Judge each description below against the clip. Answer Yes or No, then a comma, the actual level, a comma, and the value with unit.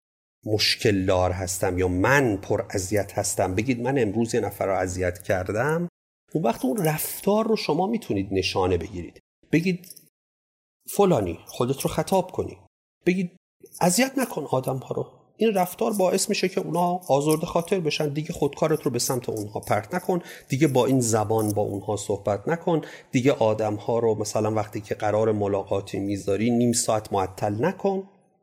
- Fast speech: Yes, fast, 160 wpm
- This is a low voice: Yes, low, 130 Hz